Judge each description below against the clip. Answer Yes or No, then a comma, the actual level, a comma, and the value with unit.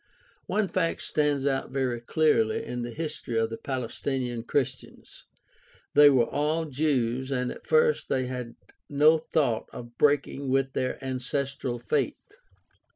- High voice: No, low, 135 Hz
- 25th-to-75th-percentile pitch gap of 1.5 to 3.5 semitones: Yes, average, 3.2 semitones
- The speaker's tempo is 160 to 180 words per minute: No, average, 145 wpm